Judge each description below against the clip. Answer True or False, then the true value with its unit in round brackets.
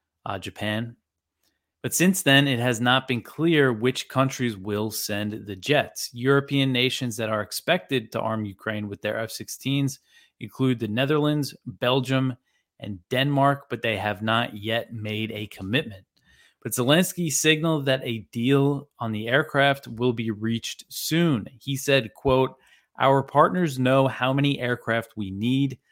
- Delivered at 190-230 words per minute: False (150 wpm)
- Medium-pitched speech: False (125 Hz)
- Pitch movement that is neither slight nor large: True (3.8 semitones)